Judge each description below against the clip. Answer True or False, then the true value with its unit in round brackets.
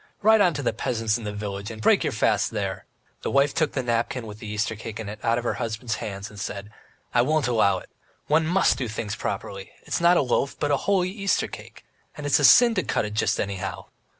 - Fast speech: True (245 wpm)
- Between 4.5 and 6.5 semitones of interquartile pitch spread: True (5.6 semitones)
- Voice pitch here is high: False (115 Hz)